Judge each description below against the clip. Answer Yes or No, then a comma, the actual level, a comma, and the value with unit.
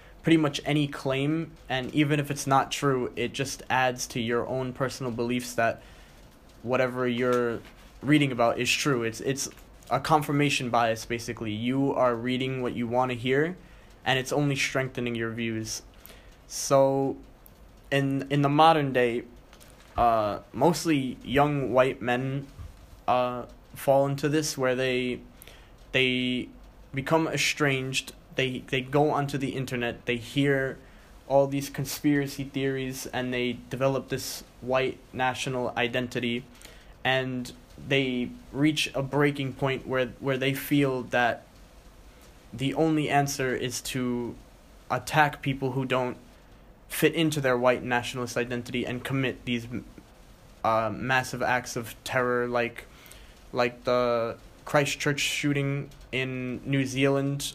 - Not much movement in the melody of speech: Yes, narrow, 2.2 semitones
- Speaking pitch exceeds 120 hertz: Yes, low, 130 Hz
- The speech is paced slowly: Yes, slow, 130 wpm